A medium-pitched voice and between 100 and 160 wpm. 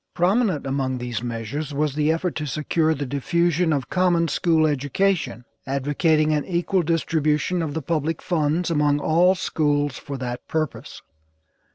Yes: medium, 155 Hz; average, 150 wpm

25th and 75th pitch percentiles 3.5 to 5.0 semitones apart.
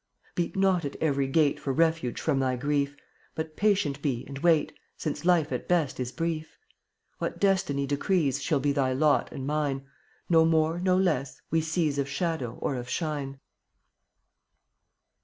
No: average, 3.1 semitones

